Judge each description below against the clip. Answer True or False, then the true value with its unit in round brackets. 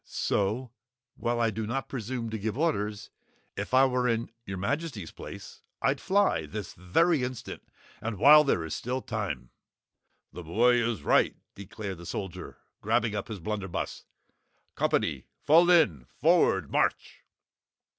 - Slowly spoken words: False (145 wpm)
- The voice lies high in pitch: False (115 Hz)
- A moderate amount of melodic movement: True (4.5 semitones)